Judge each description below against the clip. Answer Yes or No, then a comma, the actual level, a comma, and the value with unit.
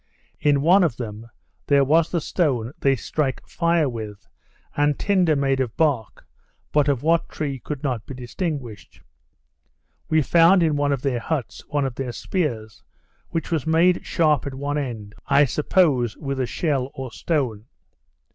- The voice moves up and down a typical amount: Yes, average, 4.2 semitones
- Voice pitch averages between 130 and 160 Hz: Yes, medium, 140 Hz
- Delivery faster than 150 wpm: Yes, average, 165 wpm